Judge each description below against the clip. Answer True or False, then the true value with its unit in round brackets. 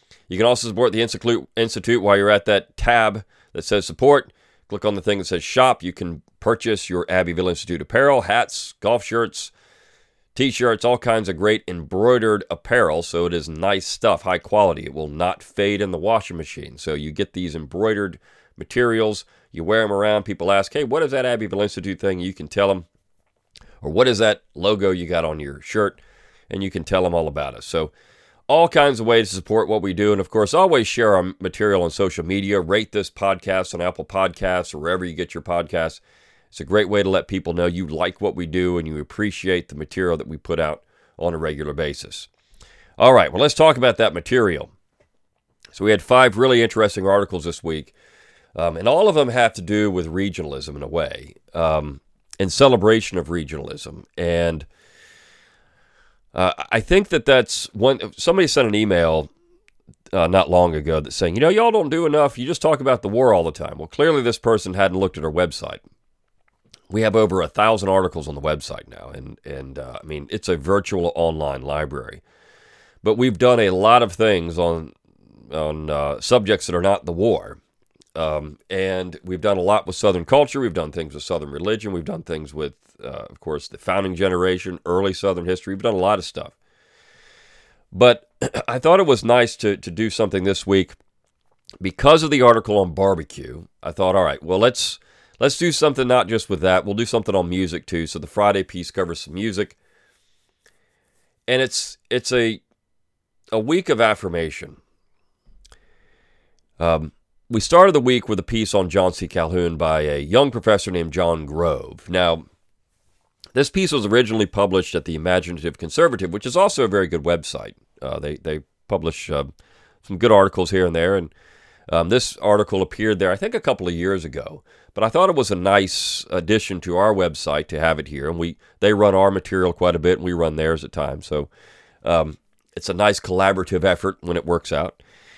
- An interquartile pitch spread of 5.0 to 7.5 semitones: False (4.2 semitones)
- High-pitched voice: False (95 Hz)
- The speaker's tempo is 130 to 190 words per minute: False (200 wpm)